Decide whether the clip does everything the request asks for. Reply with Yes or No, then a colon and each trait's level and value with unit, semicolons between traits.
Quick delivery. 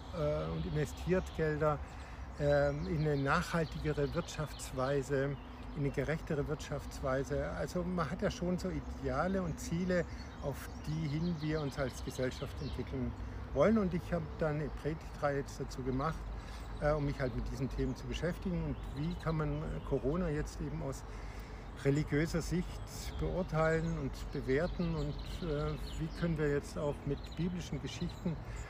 No: average, 140 wpm